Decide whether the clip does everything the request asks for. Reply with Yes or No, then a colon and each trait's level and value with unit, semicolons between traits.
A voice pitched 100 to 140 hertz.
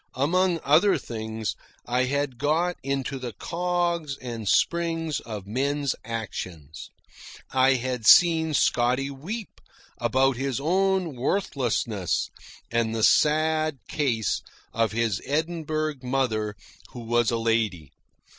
Yes: low, 135 Hz